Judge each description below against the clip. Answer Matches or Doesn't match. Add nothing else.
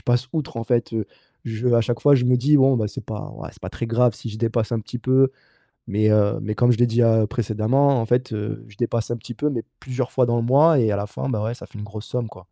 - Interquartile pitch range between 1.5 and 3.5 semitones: Matches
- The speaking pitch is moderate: Doesn't match